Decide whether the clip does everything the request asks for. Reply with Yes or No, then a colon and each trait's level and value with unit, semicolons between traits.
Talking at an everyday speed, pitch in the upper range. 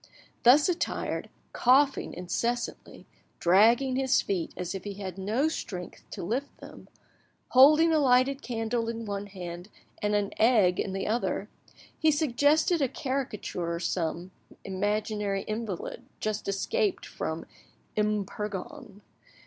No: slow, 125 wpm; high, 215 Hz